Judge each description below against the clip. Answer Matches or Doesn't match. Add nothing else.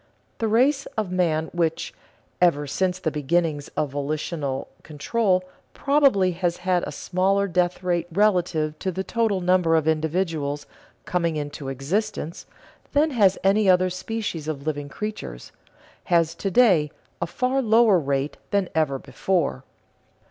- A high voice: Doesn't match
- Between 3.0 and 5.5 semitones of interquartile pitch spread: Matches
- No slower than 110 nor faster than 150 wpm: Matches